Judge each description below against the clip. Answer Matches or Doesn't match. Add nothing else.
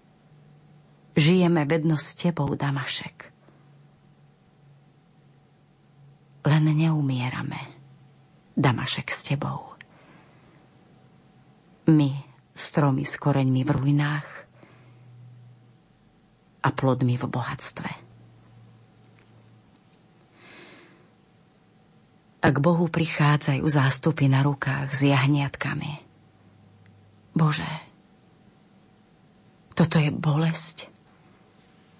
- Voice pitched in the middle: Matches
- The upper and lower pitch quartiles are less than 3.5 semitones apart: Matches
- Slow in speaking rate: Matches